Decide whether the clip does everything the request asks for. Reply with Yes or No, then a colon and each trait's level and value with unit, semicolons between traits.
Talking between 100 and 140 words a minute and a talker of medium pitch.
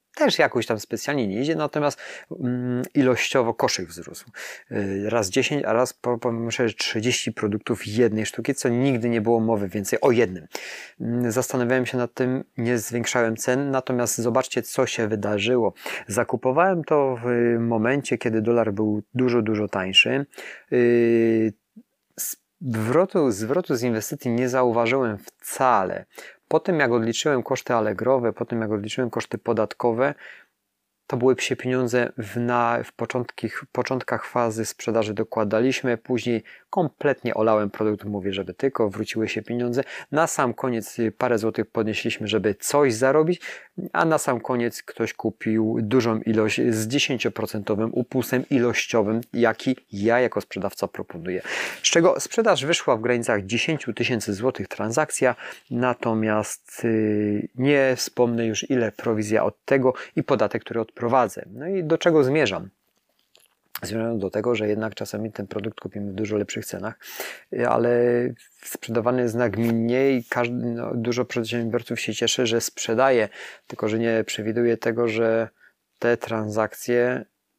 No: average, 135 wpm; low, 120 Hz